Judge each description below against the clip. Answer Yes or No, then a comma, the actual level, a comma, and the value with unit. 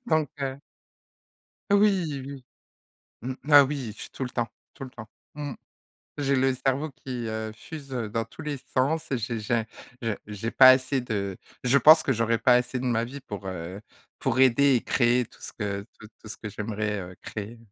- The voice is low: Yes, low, 125 Hz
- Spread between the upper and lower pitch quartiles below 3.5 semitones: No, average, 3.8 semitones